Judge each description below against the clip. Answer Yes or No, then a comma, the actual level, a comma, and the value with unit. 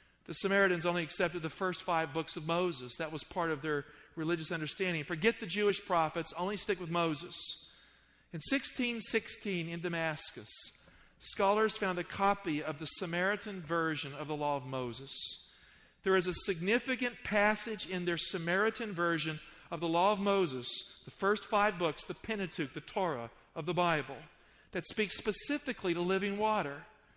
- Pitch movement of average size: Yes, average, 3.9 semitones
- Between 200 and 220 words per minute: No, average, 160 wpm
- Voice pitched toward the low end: No, medium, 175 Hz